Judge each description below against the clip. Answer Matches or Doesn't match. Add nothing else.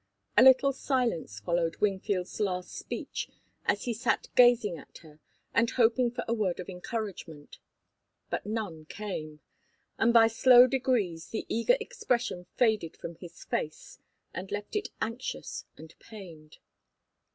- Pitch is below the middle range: Doesn't match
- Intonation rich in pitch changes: Matches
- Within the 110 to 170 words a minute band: Matches